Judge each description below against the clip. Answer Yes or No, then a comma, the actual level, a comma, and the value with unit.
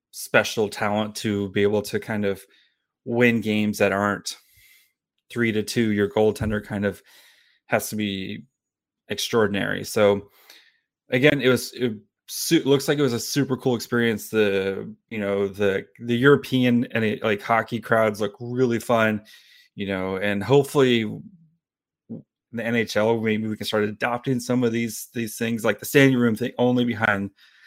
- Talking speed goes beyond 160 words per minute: No, average, 155 wpm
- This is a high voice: No, low, 115 Hz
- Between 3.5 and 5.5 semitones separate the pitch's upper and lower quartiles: No, average, 3.0 semitones